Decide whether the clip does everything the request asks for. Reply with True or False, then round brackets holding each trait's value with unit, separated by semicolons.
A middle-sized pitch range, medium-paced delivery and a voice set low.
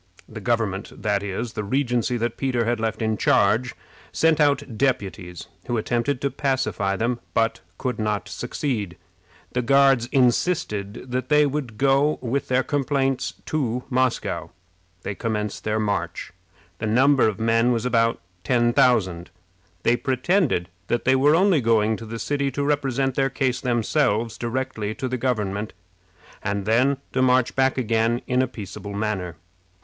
True (3.5 semitones; 155 wpm; 120 Hz)